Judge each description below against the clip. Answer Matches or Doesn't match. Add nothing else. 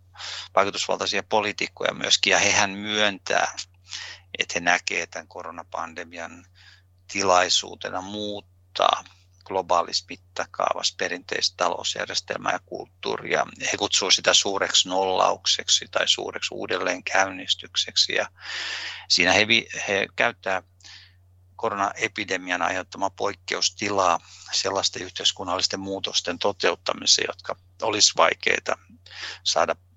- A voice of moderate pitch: Doesn't match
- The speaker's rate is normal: Doesn't match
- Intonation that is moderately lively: Doesn't match